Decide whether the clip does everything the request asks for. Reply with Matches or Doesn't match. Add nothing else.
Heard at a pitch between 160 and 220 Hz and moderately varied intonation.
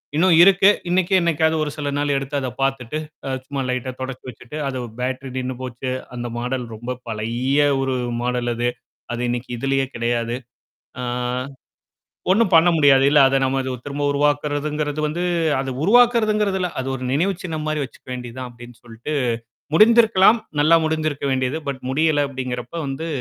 Doesn't match